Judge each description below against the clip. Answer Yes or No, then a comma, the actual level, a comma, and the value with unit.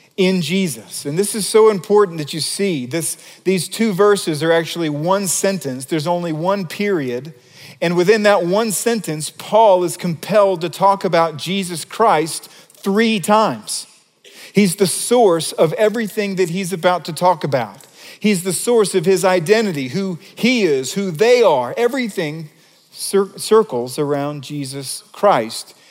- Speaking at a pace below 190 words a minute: Yes, average, 155 wpm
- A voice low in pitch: No, medium, 185 Hz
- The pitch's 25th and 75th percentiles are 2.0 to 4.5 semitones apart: Yes, average, 4.1 semitones